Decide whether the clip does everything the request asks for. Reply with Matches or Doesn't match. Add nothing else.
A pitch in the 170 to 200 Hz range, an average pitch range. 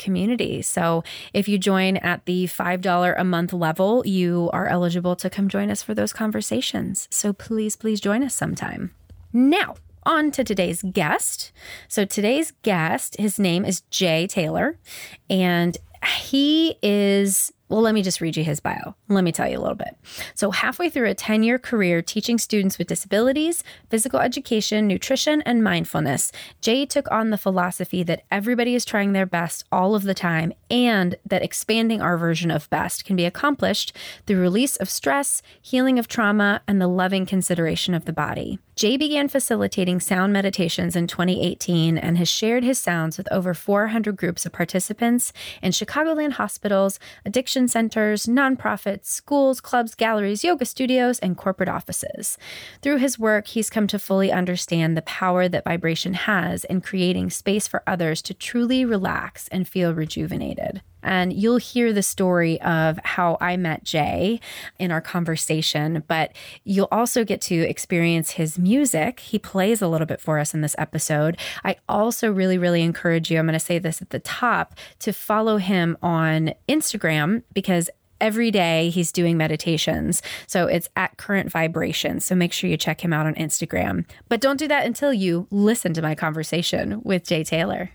Matches